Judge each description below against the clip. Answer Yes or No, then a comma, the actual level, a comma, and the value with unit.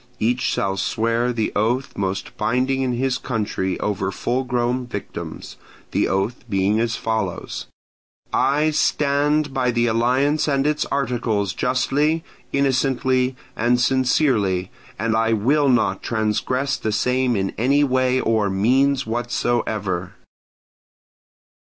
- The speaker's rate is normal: No, slow, 120 wpm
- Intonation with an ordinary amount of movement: Yes, average, 3.4 semitones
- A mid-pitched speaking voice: No, low, 120 Hz